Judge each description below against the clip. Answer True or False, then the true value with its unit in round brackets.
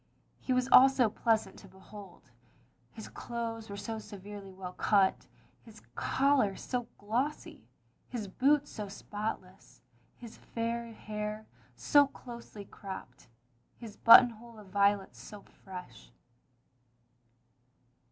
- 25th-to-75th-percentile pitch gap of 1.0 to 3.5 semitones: True (3.1 semitones)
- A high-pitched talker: True (215 Hz)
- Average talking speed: False (110 wpm)